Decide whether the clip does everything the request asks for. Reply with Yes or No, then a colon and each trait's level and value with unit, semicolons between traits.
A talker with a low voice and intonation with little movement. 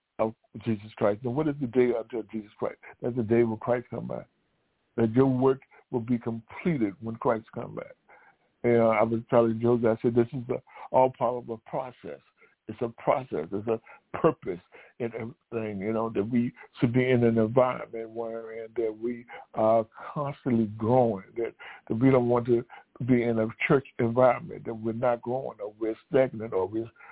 Yes: low, 120 Hz; narrow, 1.9 semitones